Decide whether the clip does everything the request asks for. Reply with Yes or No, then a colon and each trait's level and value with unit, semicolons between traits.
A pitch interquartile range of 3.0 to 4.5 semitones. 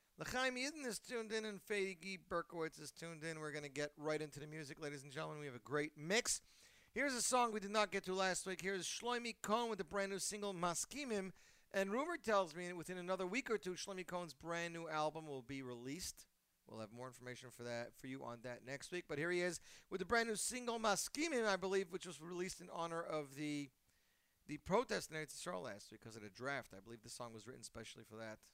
No: wide, 5.6 semitones